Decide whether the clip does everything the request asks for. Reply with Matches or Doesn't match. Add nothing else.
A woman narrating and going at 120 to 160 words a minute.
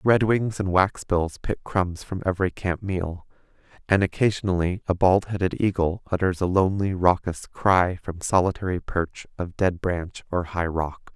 Doesn't match